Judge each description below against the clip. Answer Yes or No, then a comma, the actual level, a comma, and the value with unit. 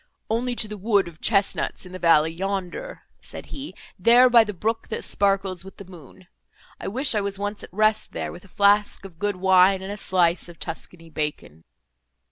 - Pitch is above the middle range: Yes, high, 195 Hz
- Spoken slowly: No, average, 200 wpm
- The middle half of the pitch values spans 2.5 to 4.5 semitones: Yes, average, 2.9 semitones